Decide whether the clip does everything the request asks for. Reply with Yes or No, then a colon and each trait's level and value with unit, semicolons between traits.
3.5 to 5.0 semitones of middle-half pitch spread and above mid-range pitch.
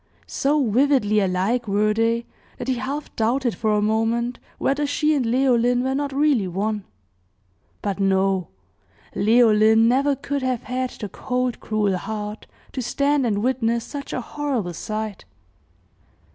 Yes: average, 3.8 semitones; high, 235 Hz